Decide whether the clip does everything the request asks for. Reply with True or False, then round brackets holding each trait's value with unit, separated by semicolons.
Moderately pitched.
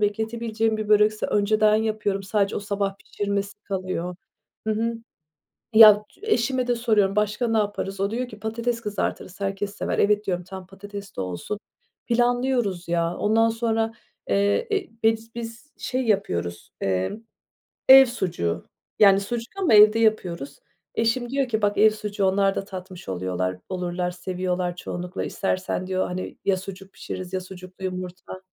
False (205 Hz)